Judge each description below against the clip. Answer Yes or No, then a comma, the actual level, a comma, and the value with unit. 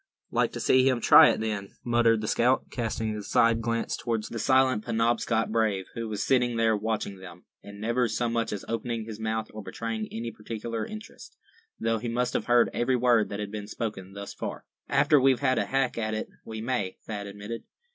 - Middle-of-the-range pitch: No, low, 115 Hz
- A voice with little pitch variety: Yes, narrow, 1.9 semitones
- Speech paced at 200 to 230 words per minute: Yes, fast, 205 wpm